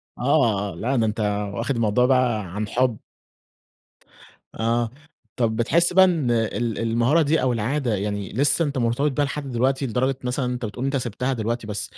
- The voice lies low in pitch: Yes, low, 120 Hz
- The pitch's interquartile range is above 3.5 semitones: No, average, 3.2 semitones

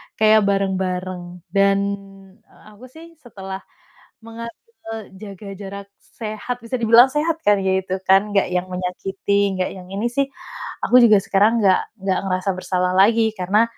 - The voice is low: No, high, 200 Hz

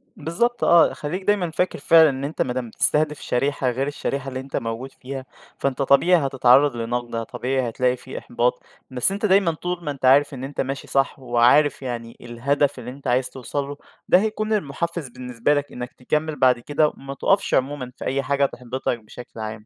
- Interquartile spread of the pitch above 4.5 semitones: No, average, 3.1 semitones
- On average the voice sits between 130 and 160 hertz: Yes, low, 135 Hz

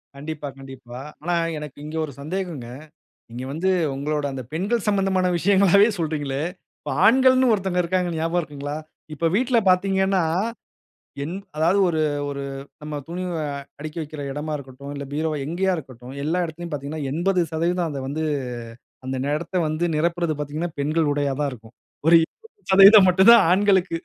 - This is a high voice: No, medium, 160 Hz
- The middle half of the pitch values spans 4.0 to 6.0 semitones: Yes, average, 4.4 semitones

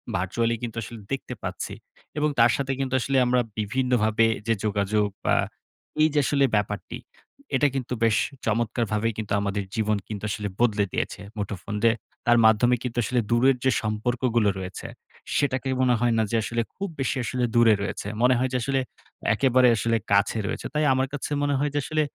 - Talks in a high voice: No, low, 120 Hz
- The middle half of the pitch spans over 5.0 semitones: No, average, 3.4 semitones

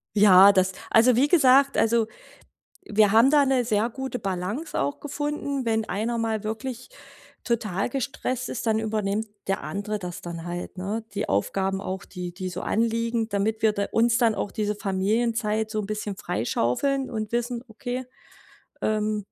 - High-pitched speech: Yes, high, 220 Hz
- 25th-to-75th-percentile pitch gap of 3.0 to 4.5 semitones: Yes, average, 3.3 semitones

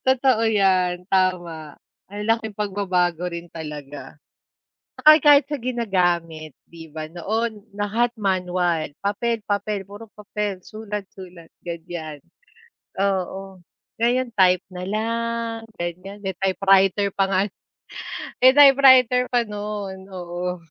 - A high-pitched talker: Yes, high, 195 Hz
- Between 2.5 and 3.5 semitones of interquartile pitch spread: No, average, 3.9 semitones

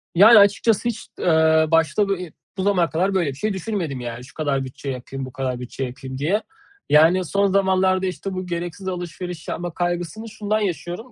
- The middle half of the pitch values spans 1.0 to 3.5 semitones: No, average, 4.6 semitones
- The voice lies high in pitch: No, medium, 175 Hz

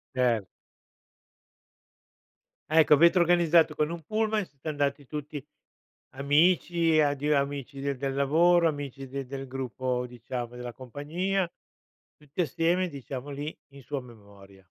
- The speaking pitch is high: No, medium, 145 Hz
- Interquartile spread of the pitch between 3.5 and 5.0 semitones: Yes, average, 3.8 semitones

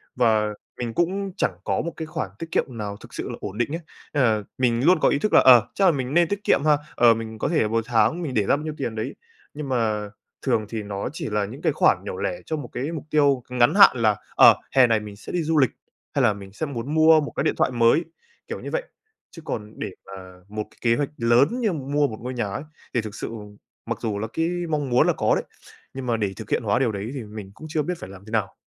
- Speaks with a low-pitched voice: Yes, low, 120 Hz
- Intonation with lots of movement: Yes, wide, 5.8 semitones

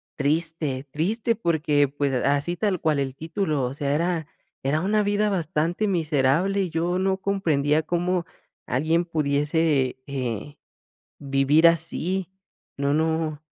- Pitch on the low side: No, medium, 160 Hz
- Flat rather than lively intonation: No, average, 3.7 semitones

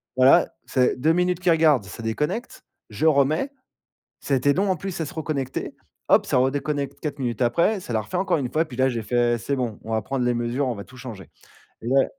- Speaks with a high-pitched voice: No, low, 135 Hz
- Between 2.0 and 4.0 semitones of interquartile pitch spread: No, average, 4.7 semitones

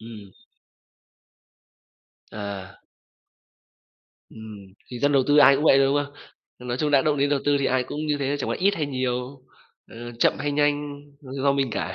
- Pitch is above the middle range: No, medium, 140 Hz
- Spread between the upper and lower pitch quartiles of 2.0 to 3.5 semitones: Yes, average, 2.8 semitones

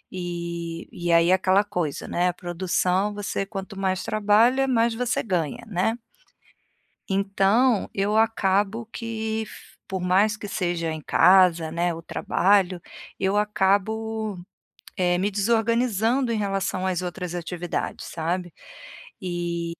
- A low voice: No, high, 195 Hz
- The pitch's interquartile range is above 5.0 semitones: No, average, 3.5 semitones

